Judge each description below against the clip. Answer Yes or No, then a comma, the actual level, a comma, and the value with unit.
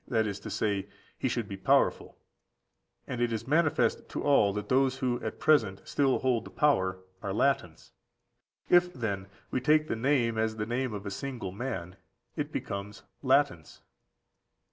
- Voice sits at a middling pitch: No, low, 115 Hz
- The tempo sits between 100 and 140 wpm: No, average, 165 wpm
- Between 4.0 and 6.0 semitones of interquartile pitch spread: Yes, average, 5.1 semitones